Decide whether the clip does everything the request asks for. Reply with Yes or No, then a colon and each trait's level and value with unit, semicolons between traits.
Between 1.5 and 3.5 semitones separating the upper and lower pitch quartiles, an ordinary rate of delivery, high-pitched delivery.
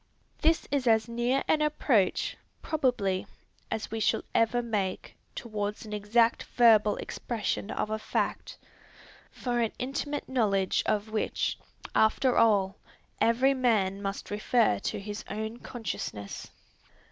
No: average, 2.9 semitones; slow, 125 wpm; high, 220 Hz